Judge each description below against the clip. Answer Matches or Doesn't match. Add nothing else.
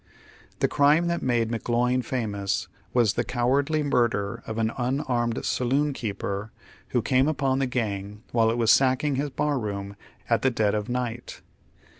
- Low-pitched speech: Matches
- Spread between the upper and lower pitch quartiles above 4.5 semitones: Doesn't match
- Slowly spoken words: Doesn't match